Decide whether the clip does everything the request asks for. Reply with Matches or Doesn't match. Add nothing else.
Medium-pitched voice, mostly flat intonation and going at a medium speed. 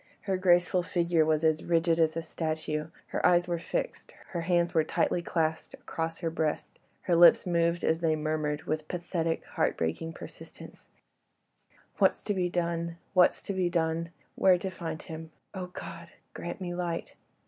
Matches